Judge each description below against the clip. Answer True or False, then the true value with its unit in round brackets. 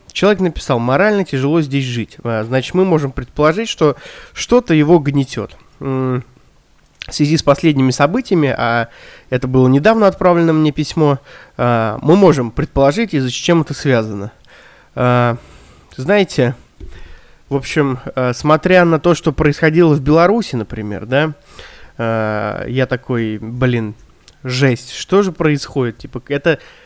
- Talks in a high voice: False (140 Hz)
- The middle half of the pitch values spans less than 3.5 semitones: False (4.7 semitones)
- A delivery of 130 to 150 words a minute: False (120 wpm)